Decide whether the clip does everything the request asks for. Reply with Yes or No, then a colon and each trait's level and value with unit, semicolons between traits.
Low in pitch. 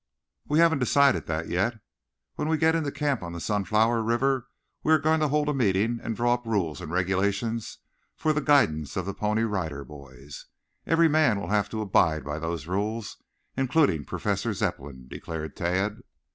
Yes: low, 105 Hz